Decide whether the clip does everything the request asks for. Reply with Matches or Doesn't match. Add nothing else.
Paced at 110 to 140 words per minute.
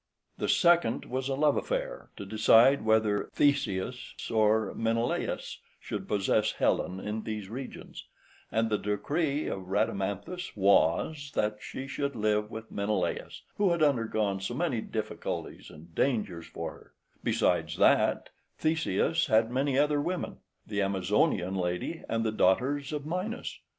Matches